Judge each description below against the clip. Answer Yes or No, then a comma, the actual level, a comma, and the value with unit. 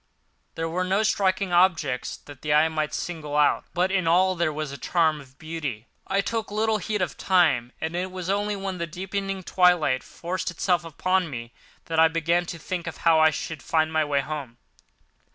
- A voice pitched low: No, medium, 170 Hz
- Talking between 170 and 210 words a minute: Yes, average, 200 wpm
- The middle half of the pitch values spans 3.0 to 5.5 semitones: Yes, average, 3.3 semitones